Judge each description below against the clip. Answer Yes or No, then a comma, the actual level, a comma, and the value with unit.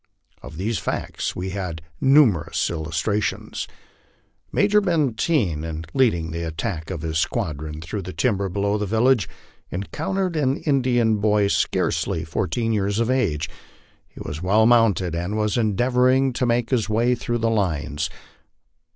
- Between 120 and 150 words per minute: Yes, average, 145 wpm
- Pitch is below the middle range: Yes, low, 105 Hz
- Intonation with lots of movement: Yes, wide, 6.4 semitones